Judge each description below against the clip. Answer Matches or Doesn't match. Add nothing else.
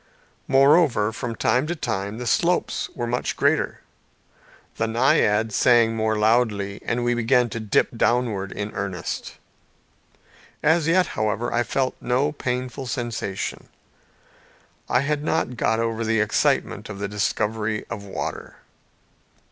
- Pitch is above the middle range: Doesn't match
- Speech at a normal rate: Doesn't match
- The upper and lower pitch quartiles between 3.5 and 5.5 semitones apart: Doesn't match